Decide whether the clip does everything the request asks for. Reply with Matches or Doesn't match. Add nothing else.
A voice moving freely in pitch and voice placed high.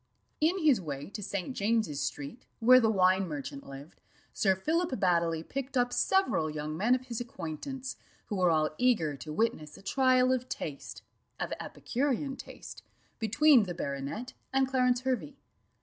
Matches